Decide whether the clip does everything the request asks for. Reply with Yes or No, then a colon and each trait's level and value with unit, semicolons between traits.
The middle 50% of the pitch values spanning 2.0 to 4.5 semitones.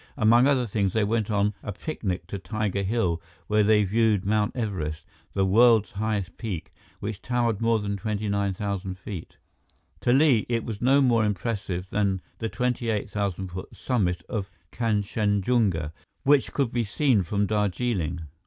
Yes: average, 2.9 semitones